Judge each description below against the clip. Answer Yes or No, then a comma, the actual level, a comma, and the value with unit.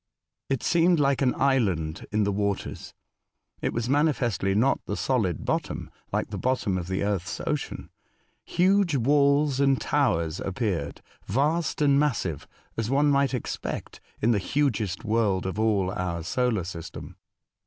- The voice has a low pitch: Yes, low, 115 Hz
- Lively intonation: Yes, wide, 6.4 semitones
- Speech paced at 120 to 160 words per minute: Yes, average, 150 wpm